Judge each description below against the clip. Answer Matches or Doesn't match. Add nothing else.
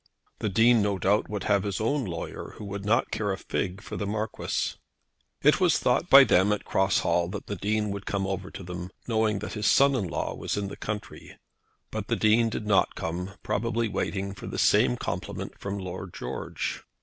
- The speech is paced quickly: Matches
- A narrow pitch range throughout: Matches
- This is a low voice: Matches